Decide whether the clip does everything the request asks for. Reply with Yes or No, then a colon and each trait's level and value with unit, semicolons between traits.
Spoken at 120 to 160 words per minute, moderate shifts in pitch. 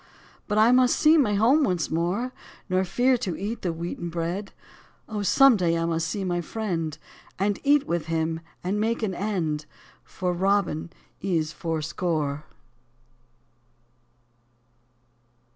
Yes: slow, 135 wpm; average, 4.5 semitones